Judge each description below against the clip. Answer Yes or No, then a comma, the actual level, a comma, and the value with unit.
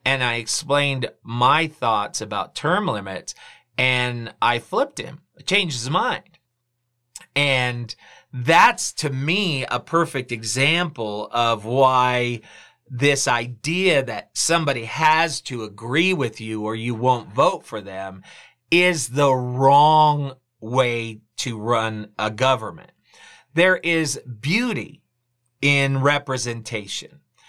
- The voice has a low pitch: Yes, low, 130 Hz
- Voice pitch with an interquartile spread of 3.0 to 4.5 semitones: Yes, average, 3.7 semitones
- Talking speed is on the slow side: Yes, slow, 115 wpm